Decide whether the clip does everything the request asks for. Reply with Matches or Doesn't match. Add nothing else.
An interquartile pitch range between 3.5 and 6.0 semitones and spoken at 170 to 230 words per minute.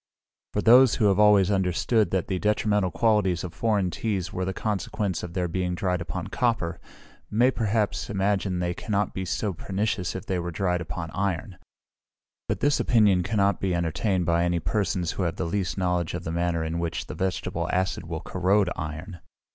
Doesn't match